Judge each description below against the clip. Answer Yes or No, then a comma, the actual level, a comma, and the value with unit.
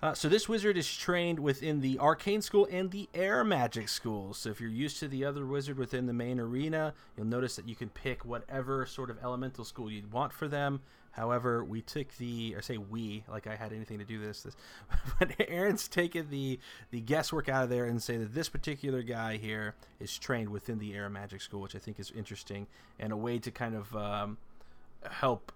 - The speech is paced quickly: Yes, fast, 220 wpm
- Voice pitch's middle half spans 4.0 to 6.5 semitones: Yes, average, 5.0 semitones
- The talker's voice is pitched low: Yes, low, 125 Hz